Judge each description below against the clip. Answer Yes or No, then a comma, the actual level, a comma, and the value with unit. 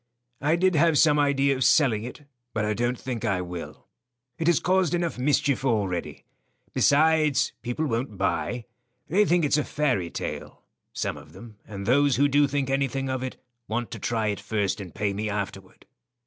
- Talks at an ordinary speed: Yes, average, 185 wpm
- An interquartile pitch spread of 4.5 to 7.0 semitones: Yes, wide, 5.5 semitones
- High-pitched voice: No, low, 130 Hz